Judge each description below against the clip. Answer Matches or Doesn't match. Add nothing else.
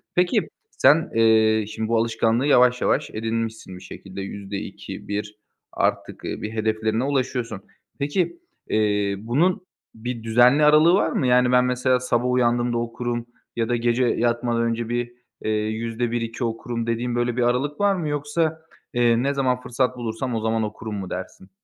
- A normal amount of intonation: Doesn't match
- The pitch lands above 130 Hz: Doesn't match